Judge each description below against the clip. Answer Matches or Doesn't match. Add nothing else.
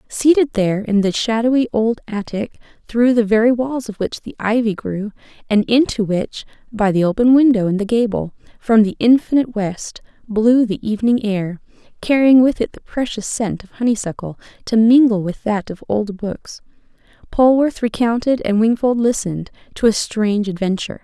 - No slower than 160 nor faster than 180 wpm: Matches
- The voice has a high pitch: Matches